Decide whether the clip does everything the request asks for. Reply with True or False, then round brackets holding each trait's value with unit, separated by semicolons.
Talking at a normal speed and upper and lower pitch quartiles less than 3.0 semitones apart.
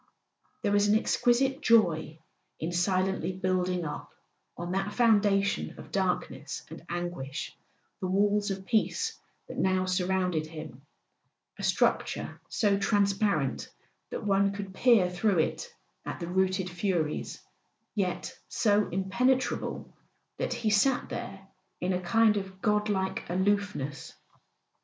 False (130 wpm; 2.5 semitones)